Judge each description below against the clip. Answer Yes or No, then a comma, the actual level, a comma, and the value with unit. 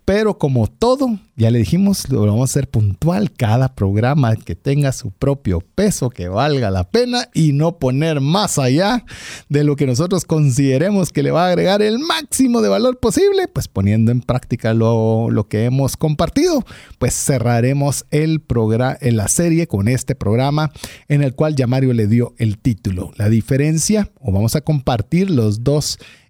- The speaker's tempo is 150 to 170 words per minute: No, average, 180 wpm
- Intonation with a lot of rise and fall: Yes, wide, 6.6 semitones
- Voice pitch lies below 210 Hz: Yes, medium, 140 Hz